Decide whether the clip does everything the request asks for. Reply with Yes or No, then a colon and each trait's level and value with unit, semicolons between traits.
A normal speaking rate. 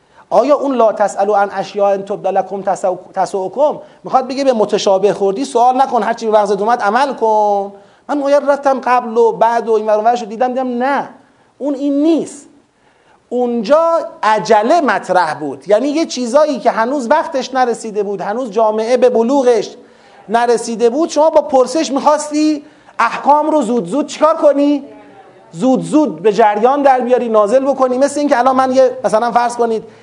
No: fast, 165 wpm